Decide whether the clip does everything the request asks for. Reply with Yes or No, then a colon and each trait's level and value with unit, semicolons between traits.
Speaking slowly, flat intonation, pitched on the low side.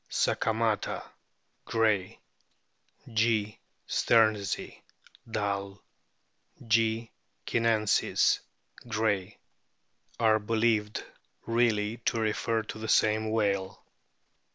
Yes: slow, 70 wpm; narrow, 1.5 semitones; low, 110 Hz